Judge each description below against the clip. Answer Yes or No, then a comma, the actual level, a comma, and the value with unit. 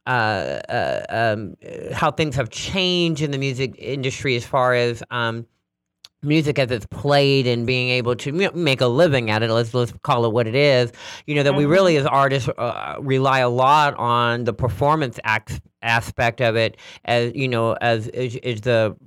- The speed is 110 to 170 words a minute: No, average, 190 wpm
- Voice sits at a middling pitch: No, low, 125 Hz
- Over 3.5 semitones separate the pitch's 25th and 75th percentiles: No, average, 3.2 semitones